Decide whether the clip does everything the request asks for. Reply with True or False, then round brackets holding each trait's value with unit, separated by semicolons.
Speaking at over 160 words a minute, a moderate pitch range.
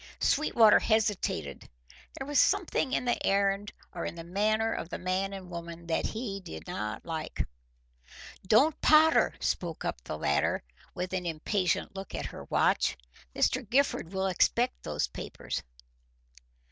False (145 wpm; 4.7 semitones)